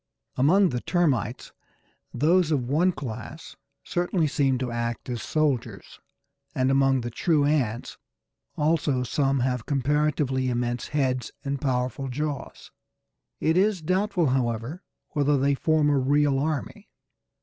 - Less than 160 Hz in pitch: Yes, medium, 140 Hz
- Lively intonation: No, average, 3.4 semitones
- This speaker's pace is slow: Yes, slow, 125 wpm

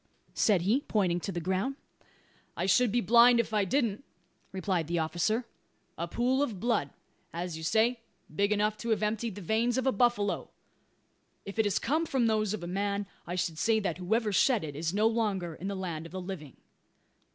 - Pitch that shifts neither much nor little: Yes, average, 4.5 semitones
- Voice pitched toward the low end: No, high, 205 Hz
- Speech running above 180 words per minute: Yes, average, 200 wpm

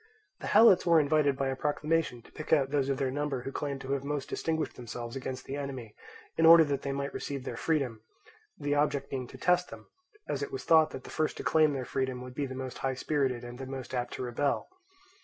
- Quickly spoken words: Yes, fast, 240 wpm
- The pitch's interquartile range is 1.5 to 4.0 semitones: Yes, narrow, 2.6 semitones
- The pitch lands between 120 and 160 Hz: Yes, medium, 140 Hz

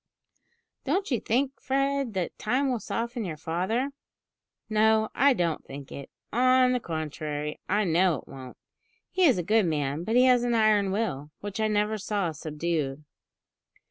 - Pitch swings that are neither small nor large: No, wide, 7.2 semitones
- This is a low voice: No, high, 210 Hz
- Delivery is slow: No, average, 165 wpm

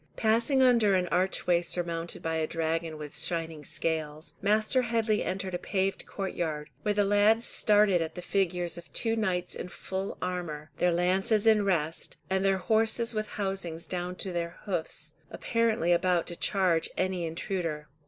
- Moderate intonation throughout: Yes, average, 3.7 semitones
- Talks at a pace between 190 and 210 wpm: No, average, 165 wpm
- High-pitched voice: No, medium, 180 Hz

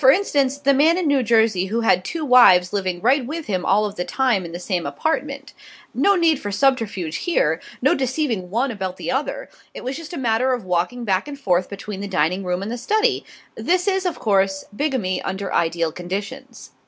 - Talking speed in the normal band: No, fast, 210 wpm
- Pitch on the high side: Yes, high, 230 Hz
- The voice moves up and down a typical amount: No, wide, 6.8 semitones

